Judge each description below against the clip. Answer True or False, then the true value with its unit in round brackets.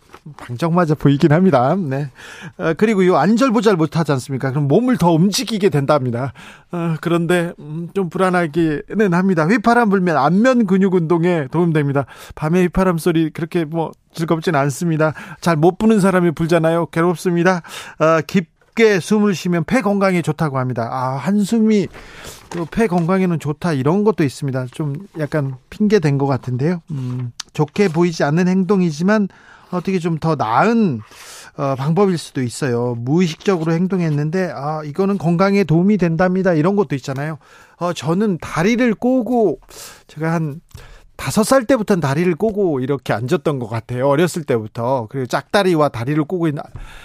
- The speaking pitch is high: False (170 Hz)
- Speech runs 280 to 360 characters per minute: True (340 characters per minute)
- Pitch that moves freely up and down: False (4.4 semitones)